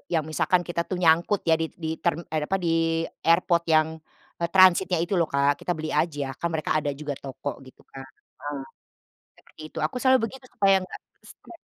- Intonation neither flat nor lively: Yes, average, 3.6 semitones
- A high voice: No, medium, 170 Hz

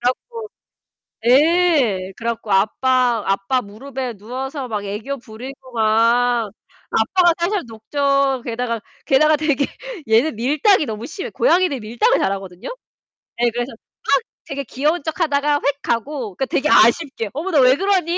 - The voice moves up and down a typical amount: Yes, average, 4.7 semitones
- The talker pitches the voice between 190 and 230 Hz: No, very high, 260 Hz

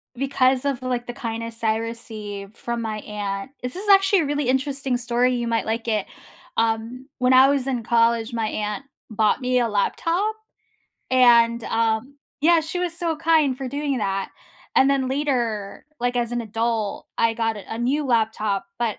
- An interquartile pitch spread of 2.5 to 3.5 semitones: Yes, average, 3.2 semitones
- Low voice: No, high, 240 Hz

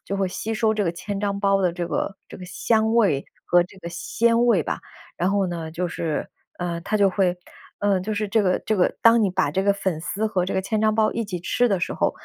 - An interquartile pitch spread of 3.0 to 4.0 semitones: Yes, average, 3.3 semitones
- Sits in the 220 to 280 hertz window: No, high, 195 Hz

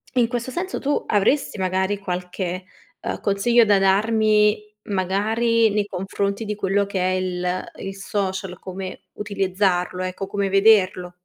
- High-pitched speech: Yes, high, 195 Hz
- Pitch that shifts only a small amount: Yes, narrow, 2.2 semitones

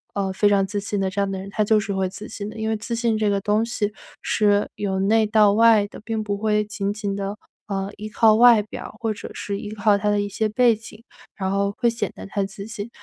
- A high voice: Yes, high, 210 Hz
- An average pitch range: No, narrow, 1.5 semitones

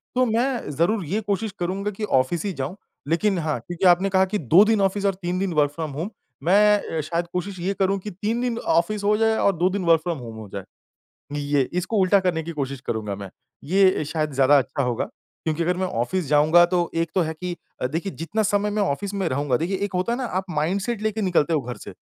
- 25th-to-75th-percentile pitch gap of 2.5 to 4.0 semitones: No, average, 4.7 semitones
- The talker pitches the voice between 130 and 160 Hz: No, medium, 180 Hz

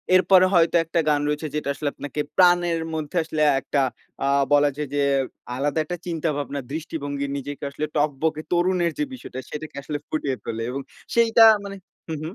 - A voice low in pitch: No, medium, 155 Hz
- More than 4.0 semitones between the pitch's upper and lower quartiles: No, average, 3.1 semitones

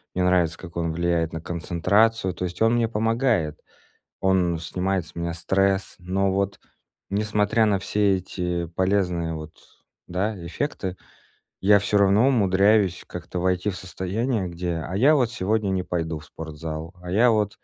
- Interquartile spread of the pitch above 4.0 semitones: No, average, 3.3 semitones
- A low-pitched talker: Yes, very low, 95 Hz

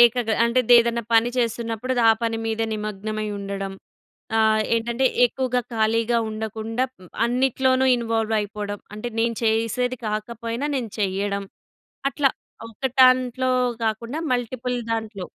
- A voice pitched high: Yes, high, 230 Hz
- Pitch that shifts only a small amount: Yes, narrow, 2.2 semitones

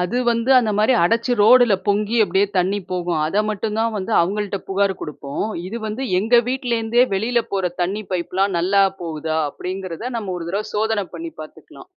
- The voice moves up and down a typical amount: Yes, average, 3.8 semitones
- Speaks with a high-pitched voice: Yes, high, 200 Hz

